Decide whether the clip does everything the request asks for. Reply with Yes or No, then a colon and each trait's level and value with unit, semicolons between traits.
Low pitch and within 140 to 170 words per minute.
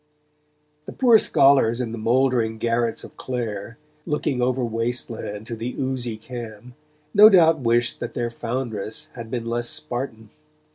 Yes: low, 120 Hz; average, 150 wpm